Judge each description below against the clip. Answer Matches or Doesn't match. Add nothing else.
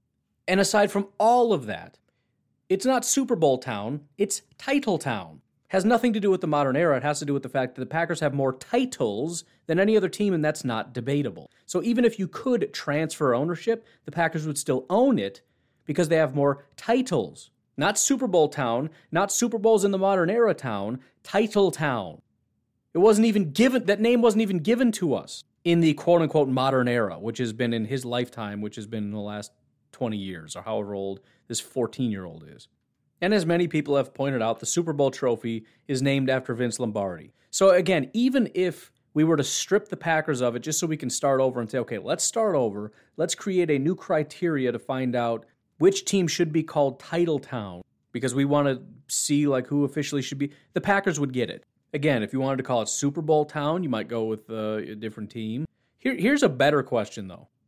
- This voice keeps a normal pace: Doesn't match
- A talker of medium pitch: Matches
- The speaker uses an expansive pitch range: Matches